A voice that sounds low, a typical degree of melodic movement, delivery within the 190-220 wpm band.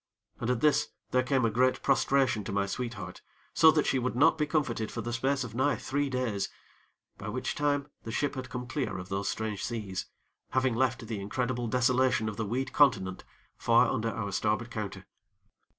Yes: low, 120 Hz; average, 3.4 semitones; average, 195 wpm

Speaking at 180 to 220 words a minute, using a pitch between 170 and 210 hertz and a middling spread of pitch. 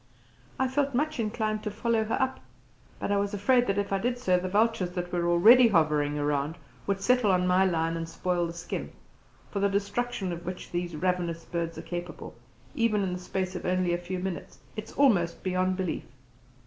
Yes: average, 200 wpm; medium, 185 Hz; average, 3.7 semitones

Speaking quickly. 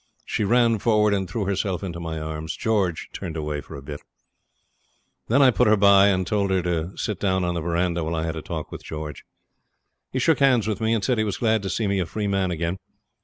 Yes: fast, 240 wpm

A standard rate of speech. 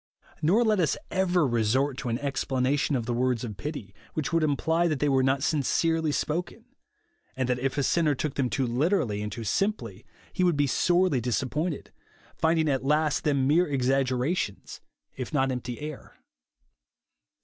Yes: average, 170 wpm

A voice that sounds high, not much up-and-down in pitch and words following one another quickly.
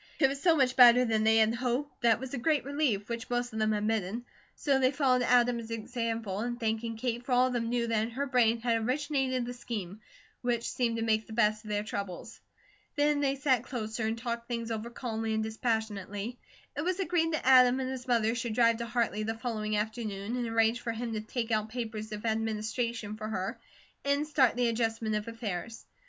Yes: high, 230 Hz; narrow, 2.3 semitones; fast, 215 wpm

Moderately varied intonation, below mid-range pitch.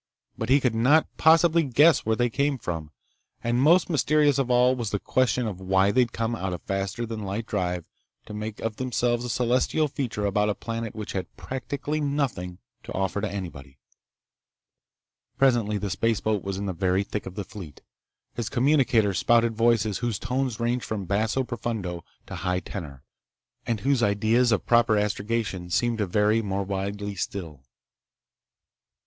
Yes: average, 3.9 semitones; low, 110 Hz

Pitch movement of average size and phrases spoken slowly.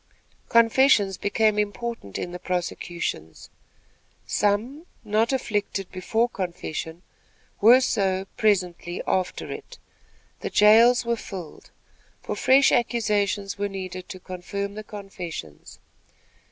Yes: average, 3.6 semitones; slow, 105 wpm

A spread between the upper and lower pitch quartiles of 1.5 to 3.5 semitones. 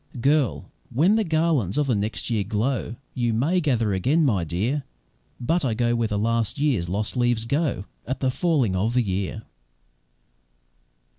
No: average, 5.3 semitones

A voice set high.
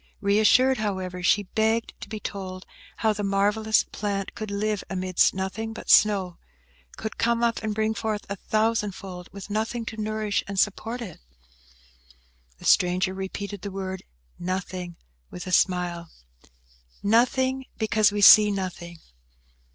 Yes: high, 205 Hz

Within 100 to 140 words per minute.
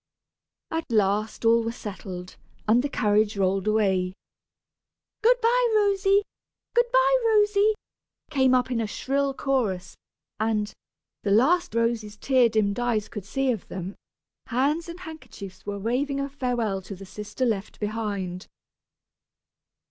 Yes: slow, 135 wpm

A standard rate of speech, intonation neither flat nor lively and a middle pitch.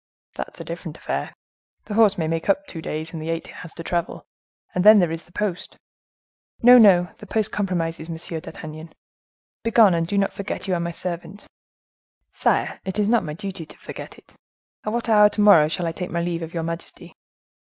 No: fast, 215 wpm; average, 3.9 semitones; medium, 175 Hz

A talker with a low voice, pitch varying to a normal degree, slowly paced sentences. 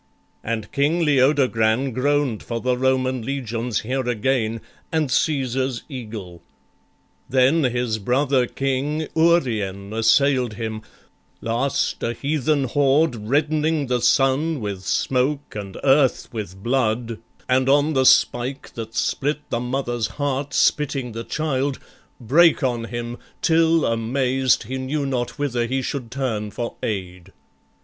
Yes: low, 130 Hz; average, 3.5 semitones; slow, 125 wpm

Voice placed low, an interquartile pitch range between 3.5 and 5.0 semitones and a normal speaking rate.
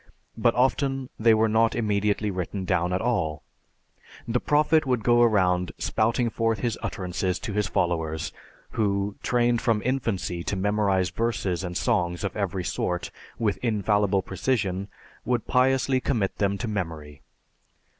Yes: low, 105 Hz; average, 4.2 semitones; average, 145 wpm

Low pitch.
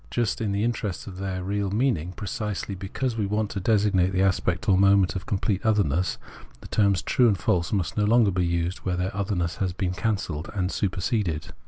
Yes: very low, 95 Hz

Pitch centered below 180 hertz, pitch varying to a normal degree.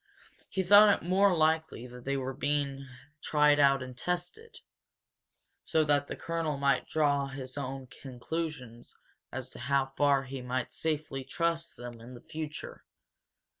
Yes: medium, 140 Hz; average, 3.4 semitones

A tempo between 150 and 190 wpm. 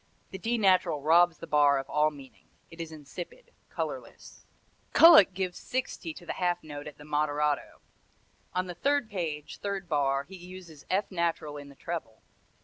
Yes: average, 170 wpm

